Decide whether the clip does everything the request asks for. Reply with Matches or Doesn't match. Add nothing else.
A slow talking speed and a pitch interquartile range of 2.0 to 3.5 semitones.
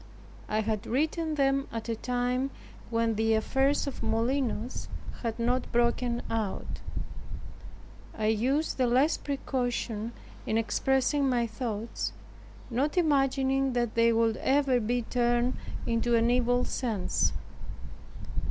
Matches